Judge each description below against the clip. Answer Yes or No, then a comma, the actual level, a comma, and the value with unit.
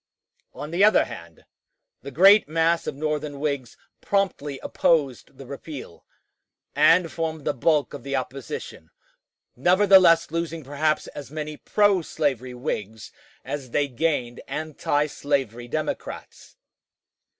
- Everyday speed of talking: No, slow, 115 wpm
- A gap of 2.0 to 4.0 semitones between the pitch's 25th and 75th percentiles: Yes, average, 3.5 semitones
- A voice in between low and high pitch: Yes, medium, 150 Hz